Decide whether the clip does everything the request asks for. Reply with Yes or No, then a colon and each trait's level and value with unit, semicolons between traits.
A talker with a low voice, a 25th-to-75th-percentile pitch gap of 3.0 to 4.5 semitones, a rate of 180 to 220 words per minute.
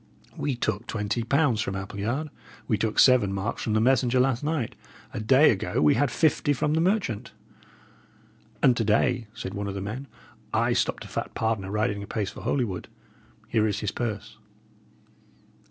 No: low, 115 Hz; average, 4.1 semitones; average, 170 wpm